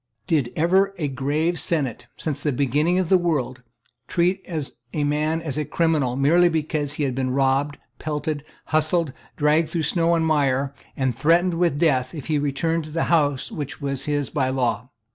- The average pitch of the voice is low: No, medium, 150 Hz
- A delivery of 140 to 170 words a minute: No, average, 180 wpm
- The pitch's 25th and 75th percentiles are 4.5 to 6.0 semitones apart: No, average, 3.3 semitones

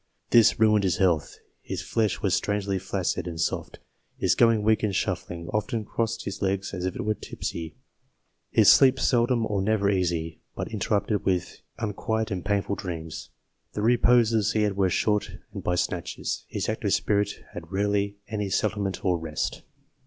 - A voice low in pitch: Yes, low, 100 Hz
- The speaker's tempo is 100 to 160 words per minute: No, average, 170 wpm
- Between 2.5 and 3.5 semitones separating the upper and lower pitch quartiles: Yes, average, 2.8 semitones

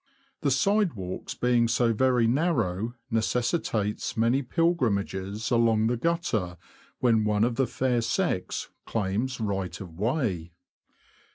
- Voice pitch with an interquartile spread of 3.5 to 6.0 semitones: Yes, average, 4.1 semitones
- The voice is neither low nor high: No, low, 115 Hz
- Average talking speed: No, slow, 125 wpm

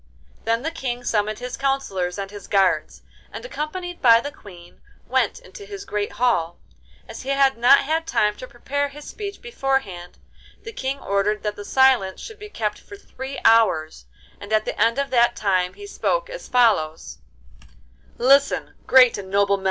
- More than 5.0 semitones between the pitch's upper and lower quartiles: Yes, wide, 5.5 semitones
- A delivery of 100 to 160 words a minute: No, average, 170 wpm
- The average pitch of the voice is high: Yes, high, 240 Hz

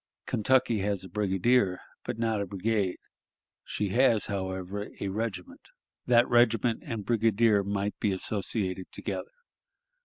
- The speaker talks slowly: Yes, slow, 125 wpm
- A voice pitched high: No, low, 105 Hz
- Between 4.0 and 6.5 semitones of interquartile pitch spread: No, average, 3.1 semitones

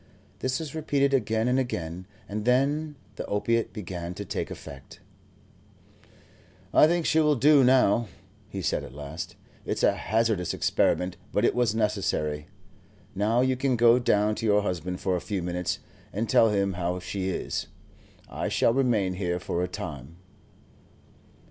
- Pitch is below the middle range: Yes, low, 105 Hz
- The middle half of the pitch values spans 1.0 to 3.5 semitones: No, wide, 5.6 semitones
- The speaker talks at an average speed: Yes, average, 160 wpm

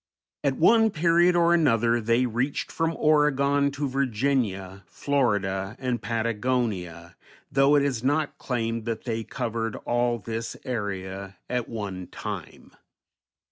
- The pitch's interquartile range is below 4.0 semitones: No, average, 4.6 semitones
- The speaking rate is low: Yes, slow, 125 wpm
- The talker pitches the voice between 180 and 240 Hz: No, low, 120 Hz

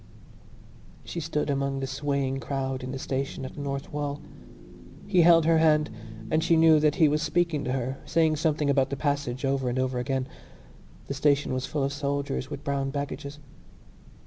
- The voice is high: No, medium, 140 Hz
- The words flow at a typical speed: Yes, average, 185 wpm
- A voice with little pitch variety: Yes, narrow, 2.0 semitones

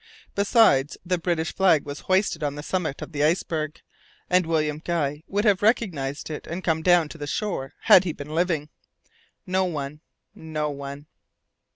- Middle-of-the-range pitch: Yes, medium, 160 Hz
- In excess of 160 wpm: Yes, average, 170 wpm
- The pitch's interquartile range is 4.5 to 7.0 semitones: No, average, 3.8 semitones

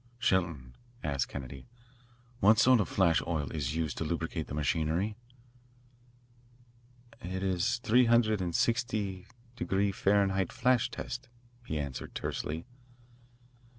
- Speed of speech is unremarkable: No, slow, 120 wpm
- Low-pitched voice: Yes, very low, 95 Hz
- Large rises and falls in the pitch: Yes, wide, 6.0 semitones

